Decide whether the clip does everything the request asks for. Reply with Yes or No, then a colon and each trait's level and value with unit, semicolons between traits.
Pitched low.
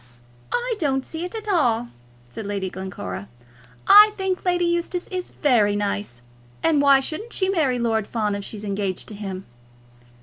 No: high, 245 Hz